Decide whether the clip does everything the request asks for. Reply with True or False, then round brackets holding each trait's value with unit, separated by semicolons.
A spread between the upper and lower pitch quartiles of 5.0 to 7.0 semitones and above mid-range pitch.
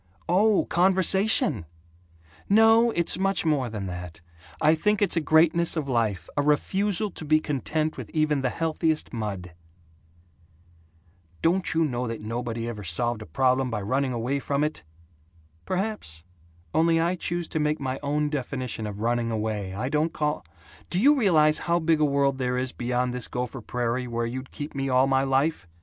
False (5.5 semitones; 140 Hz)